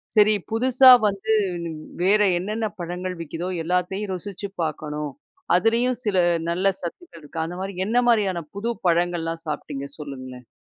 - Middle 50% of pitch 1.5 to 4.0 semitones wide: No, average, 4.4 semitones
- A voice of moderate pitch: Yes, medium, 180 Hz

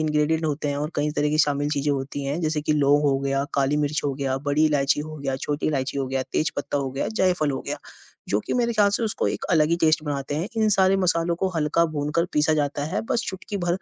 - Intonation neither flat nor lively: No, narrow, 2.2 semitones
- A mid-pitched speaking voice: Yes, medium, 150 Hz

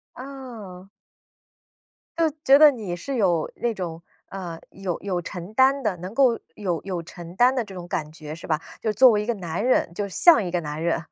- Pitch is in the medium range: No, high, 195 Hz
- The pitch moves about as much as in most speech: No, wide, 5.8 semitones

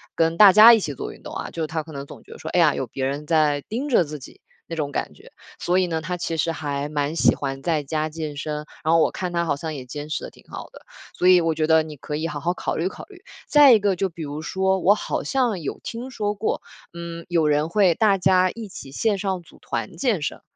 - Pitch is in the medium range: Yes, medium, 165 Hz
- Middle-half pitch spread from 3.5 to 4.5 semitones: Yes, average, 4.0 semitones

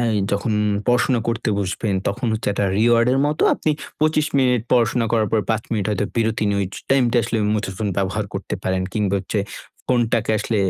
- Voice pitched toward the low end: Yes, low, 110 Hz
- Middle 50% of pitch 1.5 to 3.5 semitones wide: Yes, average, 2.8 semitones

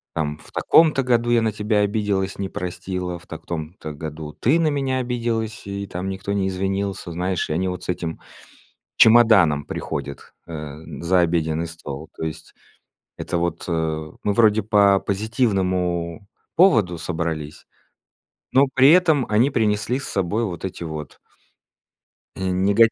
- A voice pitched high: No, very low, 95 Hz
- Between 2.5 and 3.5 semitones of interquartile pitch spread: No, average, 4.7 semitones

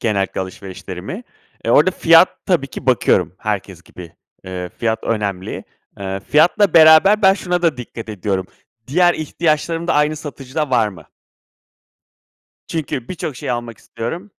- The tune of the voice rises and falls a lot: Yes, wide, 8.8 semitones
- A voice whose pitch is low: Yes, low, 130 Hz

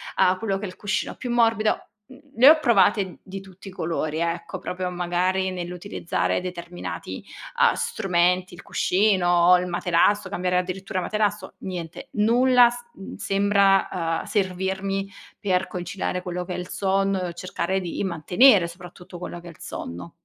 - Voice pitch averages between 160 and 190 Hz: Yes, medium, 185 Hz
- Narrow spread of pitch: Yes, narrow, 2.1 semitones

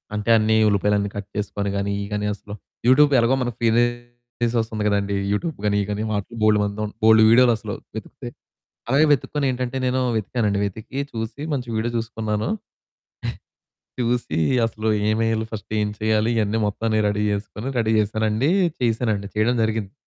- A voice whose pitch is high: No, low, 110 Hz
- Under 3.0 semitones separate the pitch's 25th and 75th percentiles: Yes, narrow, 2.5 semitones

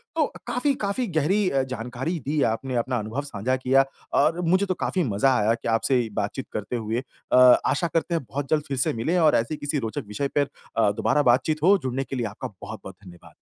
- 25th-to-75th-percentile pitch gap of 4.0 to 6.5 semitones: Yes, wide, 5.4 semitones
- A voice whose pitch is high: No, low, 135 Hz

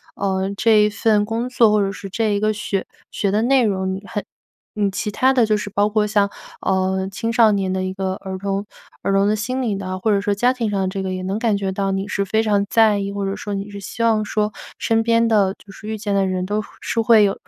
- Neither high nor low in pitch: No, high, 205 Hz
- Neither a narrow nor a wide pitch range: No, narrow, 2.0 semitones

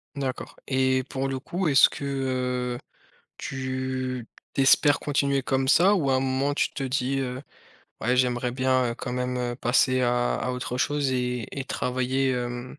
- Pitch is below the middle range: Yes, low, 130 Hz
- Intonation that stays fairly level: Yes, narrow, 1.4 semitones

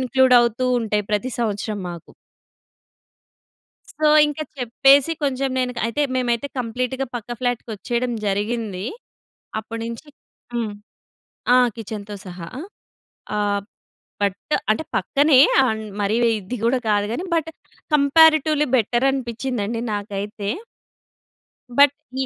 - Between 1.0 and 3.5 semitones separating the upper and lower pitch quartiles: No, average, 4.0 semitones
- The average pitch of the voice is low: No, high, 235 Hz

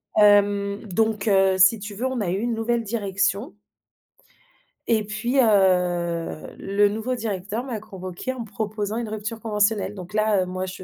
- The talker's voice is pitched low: No, high, 205 Hz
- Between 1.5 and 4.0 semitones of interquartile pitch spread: Yes, narrow, 2.5 semitones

